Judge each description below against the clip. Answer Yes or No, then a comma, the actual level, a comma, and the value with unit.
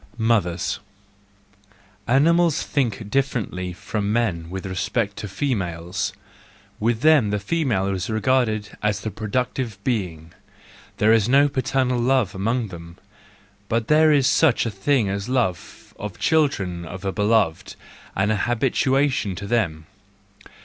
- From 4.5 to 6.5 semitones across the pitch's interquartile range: Yes, average, 5.2 semitones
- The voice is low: Yes, low, 110 Hz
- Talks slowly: Yes, slow, 130 wpm